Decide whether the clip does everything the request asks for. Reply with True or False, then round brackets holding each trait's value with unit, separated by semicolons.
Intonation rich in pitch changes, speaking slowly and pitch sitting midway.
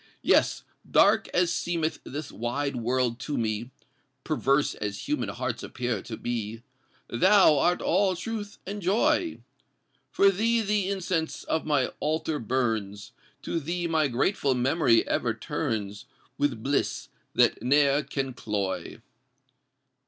True (7.0 semitones; 125 wpm; 145 Hz)